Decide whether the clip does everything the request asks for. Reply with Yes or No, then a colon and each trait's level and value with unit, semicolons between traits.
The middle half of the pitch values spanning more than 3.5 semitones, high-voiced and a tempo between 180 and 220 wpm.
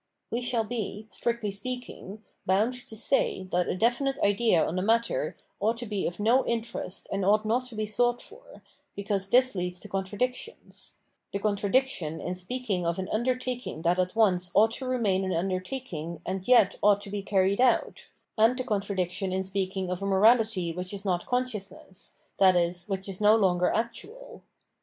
Yes: average, 4.1 semitones; high, 205 Hz; average, 185 wpm